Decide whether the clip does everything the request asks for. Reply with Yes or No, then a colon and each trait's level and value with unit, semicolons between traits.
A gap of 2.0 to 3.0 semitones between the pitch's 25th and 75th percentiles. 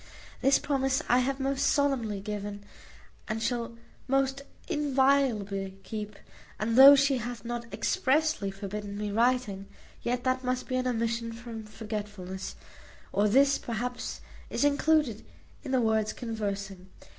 No: average, 4.2 semitones